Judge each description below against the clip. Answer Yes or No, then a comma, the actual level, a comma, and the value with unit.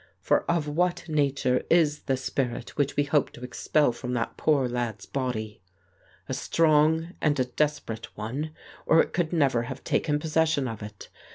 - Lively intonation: No, average, 4.0 semitones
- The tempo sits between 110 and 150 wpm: No, average, 170 wpm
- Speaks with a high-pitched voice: No, medium, 140 Hz